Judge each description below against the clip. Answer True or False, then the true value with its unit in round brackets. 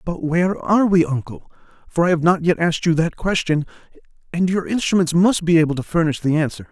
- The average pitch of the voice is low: False (170 Hz)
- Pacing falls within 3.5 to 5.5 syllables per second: False (6.1 syllables/s)